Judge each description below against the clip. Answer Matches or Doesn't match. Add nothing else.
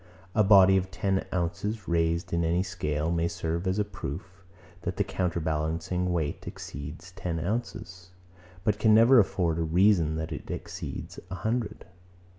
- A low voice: Matches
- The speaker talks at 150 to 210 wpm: Matches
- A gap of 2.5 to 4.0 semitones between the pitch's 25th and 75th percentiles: Matches